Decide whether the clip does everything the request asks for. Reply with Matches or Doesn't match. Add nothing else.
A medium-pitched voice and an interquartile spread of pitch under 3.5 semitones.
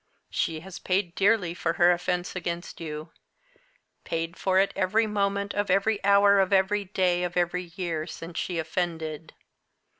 Matches